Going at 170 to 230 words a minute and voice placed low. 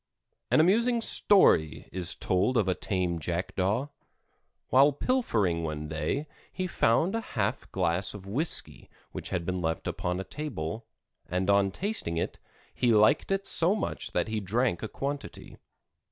No: average, 155 wpm; low, 105 Hz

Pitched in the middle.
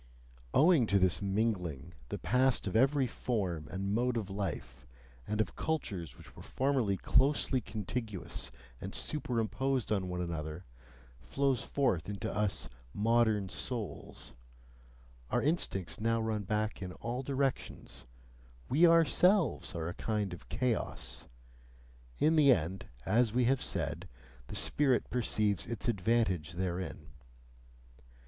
No: low, 110 Hz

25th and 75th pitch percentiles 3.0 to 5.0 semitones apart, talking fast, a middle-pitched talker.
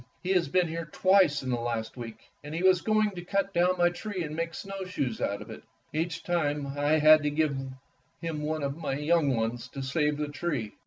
Yes: average, 4.0 semitones; fast, 220 wpm; medium, 155 Hz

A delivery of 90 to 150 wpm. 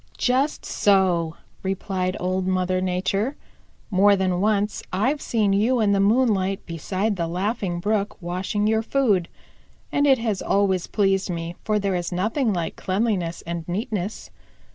Yes: average, 145 wpm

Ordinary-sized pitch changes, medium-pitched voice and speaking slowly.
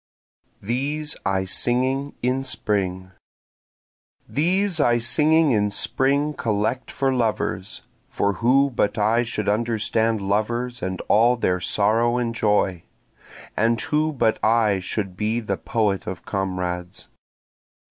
No: average, 4.1 semitones; low, 115 Hz; slow, 120 wpm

